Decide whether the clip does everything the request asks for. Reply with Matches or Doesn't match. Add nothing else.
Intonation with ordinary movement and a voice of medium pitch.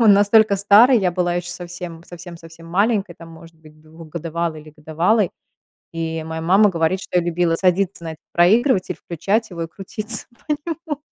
Matches